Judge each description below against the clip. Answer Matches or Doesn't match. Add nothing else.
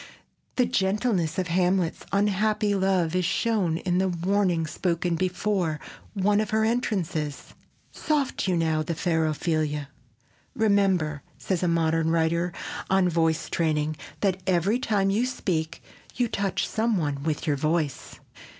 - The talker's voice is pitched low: Doesn't match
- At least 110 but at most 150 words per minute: Matches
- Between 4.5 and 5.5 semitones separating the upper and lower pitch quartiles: Doesn't match